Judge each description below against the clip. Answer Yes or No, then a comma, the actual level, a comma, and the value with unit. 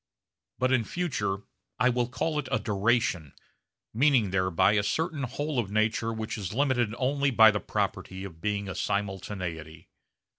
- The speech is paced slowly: No, average, 155 wpm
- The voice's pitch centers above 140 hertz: No, low, 110 Hz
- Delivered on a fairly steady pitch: No, average, 4.7 semitones